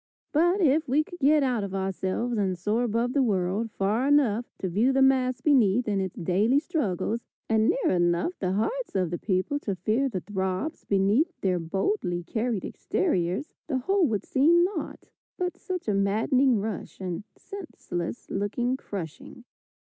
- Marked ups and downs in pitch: Yes, wide, 6.3 semitones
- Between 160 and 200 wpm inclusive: Yes, average, 165 wpm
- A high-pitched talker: Yes, high, 225 Hz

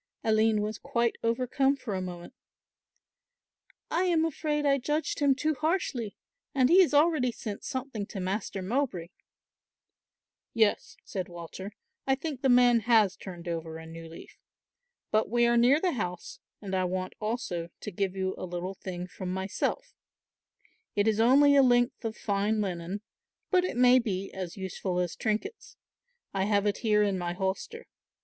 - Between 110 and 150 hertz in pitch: No, high, 215 Hz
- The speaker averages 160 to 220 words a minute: Yes, average, 165 wpm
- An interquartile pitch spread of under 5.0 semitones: No, wide, 5.6 semitones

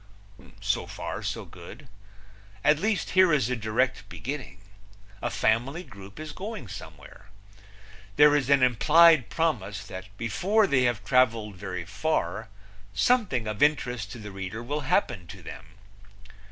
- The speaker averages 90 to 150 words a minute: Yes, average, 140 wpm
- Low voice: Yes, low, 125 Hz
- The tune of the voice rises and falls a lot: Yes, wide, 6.5 semitones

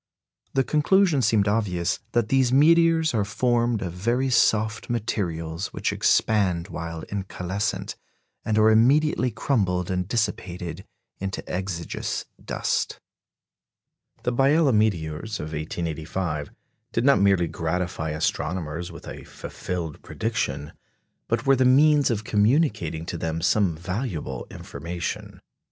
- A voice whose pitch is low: Yes, low, 100 Hz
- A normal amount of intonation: No, wide, 5.9 semitones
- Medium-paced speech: No, slow, 120 wpm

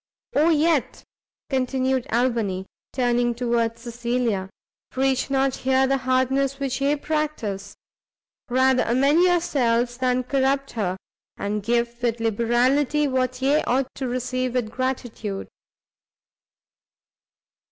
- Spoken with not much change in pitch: Yes, narrow, 2.3 semitones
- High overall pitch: Yes, very high, 255 Hz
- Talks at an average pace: No, slow, 110 wpm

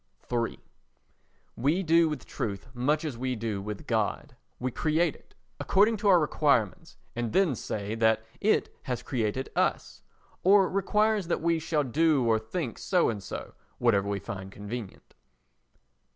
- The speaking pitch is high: No, low, 130 Hz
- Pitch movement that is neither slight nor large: No, wide, 7.0 semitones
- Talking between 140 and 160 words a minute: Yes, average, 150 wpm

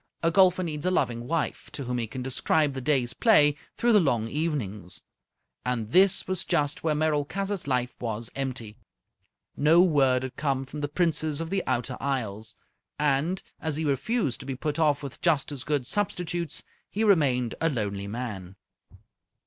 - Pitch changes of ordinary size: Yes, average, 4.7 semitones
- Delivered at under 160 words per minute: No, average, 175 wpm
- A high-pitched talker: No, medium, 145 Hz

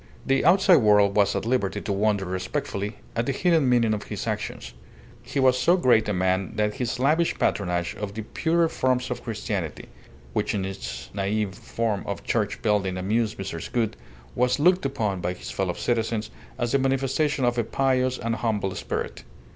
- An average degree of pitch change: Yes, average, 4.5 semitones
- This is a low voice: Yes, low, 110 Hz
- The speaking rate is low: No, average, 180 wpm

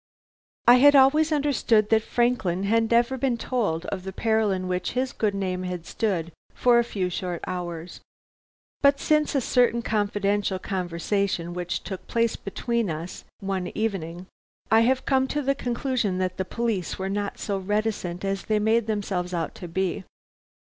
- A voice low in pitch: No, high, 205 Hz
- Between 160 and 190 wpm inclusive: Yes, average, 170 wpm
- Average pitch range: Yes, average, 4.5 semitones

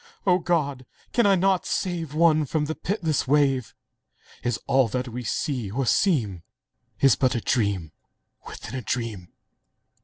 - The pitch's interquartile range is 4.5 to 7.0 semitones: Yes, wide, 5.6 semitones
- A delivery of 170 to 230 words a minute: No, average, 145 wpm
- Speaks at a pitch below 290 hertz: Yes, low, 135 Hz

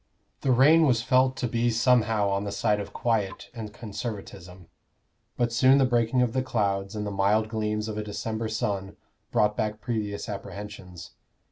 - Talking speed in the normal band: Yes, average, 170 wpm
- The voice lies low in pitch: Yes, low, 110 Hz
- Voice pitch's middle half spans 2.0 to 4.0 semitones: Yes, average, 2.8 semitones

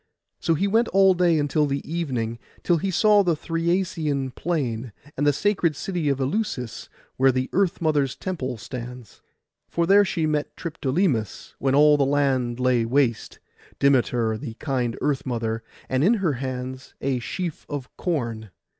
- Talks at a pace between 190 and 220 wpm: No, average, 160 wpm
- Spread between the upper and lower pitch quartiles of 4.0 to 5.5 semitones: Yes, average, 5.2 semitones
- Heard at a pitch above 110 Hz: Yes, medium, 140 Hz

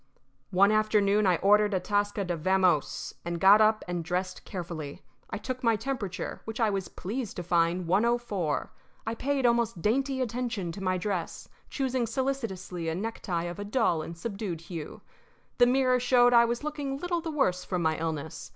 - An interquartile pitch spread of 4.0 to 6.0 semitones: Yes, average, 5.2 semitones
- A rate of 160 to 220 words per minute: Yes, average, 180 wpm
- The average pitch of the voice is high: Yes, high, 205 Hz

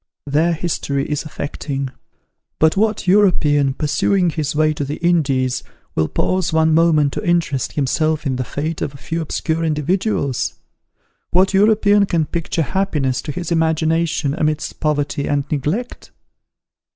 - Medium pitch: Yes, medium, 155 Hz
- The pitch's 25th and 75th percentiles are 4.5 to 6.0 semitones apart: No, average, 3.1 semitones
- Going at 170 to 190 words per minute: No, average, 140 wpm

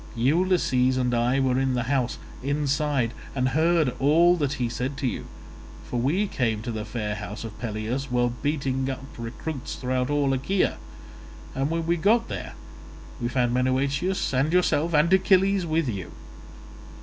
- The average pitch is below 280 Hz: Yes, low, 135 Hz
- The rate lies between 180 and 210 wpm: No, average, 160 wpm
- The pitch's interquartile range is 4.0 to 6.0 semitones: Yes, average, 4.3 semitones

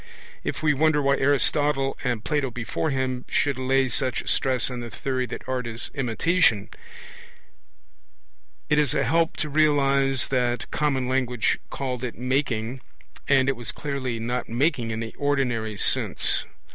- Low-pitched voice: Yes, low, 130 Hz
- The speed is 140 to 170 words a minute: Yes, average, 150 wpm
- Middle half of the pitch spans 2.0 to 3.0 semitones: Yes, average, 2.7 semitones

